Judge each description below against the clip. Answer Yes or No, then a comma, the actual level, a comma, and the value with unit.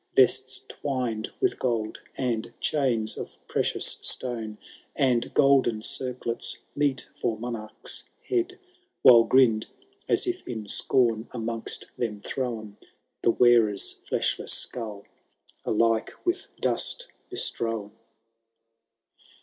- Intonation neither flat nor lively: Yes, average, 3.0 semitones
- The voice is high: No, low, 120 Hz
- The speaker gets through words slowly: Yes, slow, 100 wpm